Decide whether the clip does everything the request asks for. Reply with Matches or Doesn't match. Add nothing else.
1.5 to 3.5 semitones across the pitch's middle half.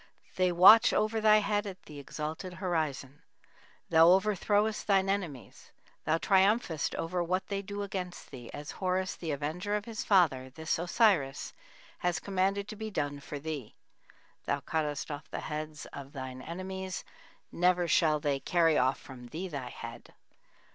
Doesn't match